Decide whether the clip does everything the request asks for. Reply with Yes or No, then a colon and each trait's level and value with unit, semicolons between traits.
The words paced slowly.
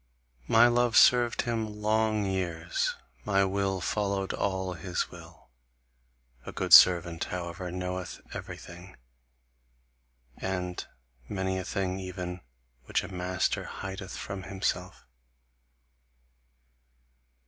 Yes: slow, 100 wpm